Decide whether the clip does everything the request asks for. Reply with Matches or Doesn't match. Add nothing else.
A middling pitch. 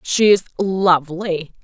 Matches